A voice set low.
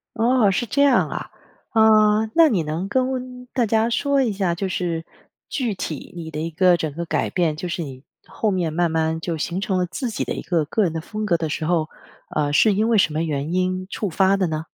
No: medium, 185 Hz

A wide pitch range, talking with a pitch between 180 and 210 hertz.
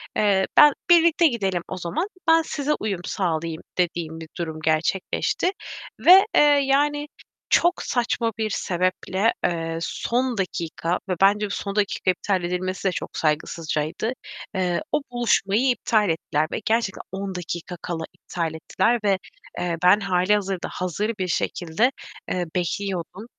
No: average, 4.8 semitones; high, 190 Hz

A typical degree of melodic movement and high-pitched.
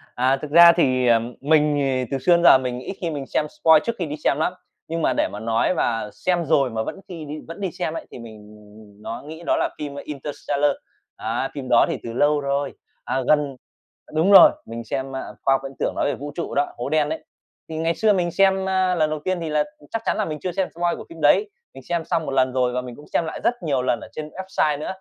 No: average, 4.4 semitones; medium, 150 Hz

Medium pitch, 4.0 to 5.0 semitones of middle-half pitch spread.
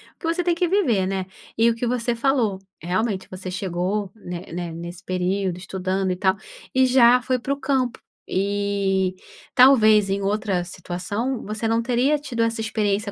No: high, 205 Hz; average, 4.6 semitones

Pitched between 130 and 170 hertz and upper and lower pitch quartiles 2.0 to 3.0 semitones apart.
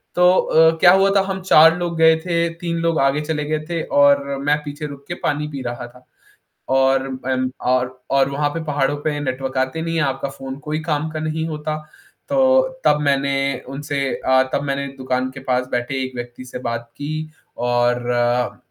No: medium, 140 Hz; average, 3.5 semitones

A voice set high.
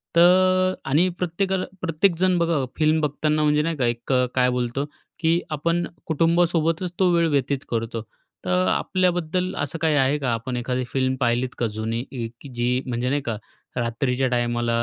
No: medium, 145 Hz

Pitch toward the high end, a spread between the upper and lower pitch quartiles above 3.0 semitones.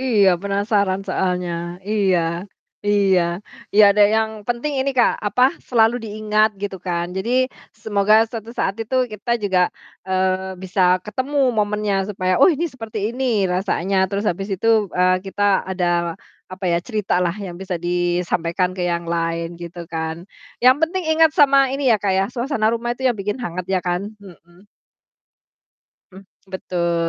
Yes: high, 195 Hz; average, 3.6 semitones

